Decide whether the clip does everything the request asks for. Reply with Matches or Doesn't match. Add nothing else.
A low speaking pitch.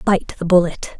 Doesn't match